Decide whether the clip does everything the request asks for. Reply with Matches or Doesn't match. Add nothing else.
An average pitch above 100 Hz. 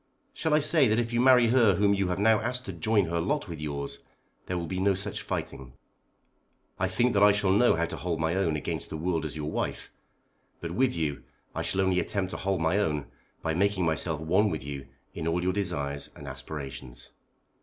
Doesn't match